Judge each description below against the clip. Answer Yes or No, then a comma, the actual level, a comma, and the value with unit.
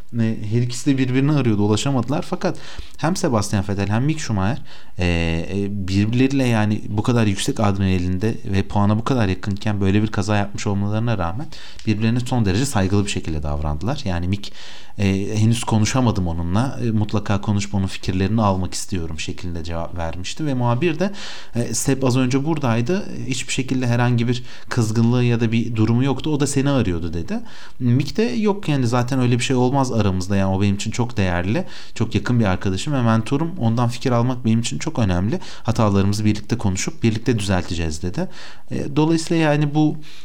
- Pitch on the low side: Yes, low, 115 Hz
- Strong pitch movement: No, average, 4.7 semitones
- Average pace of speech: No, fast, 170 wpm